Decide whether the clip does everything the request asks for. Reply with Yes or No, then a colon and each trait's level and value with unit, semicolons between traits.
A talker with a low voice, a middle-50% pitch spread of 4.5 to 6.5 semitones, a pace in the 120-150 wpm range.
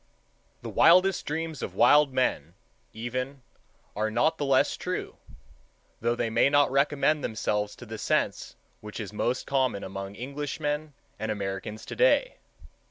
Yes: low, 130 Hz; wide, 5.4 semitones; average, 145 wpm